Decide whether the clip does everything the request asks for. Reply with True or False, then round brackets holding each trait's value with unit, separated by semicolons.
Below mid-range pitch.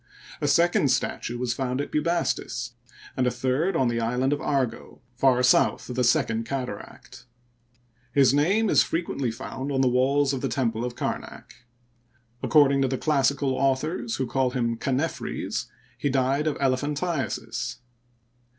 True (130 Hz)